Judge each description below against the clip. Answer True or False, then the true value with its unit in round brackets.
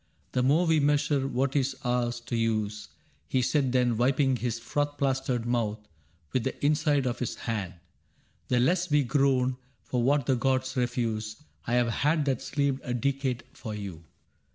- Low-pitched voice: True (130 Hz)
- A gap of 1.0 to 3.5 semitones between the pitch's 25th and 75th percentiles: True (2.7 semitones)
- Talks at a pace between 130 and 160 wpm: False (175 wpm)